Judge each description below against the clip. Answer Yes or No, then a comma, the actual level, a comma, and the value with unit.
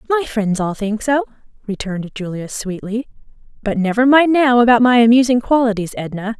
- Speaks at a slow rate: No, average, 160 wpm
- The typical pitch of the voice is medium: No, high, 230 Hz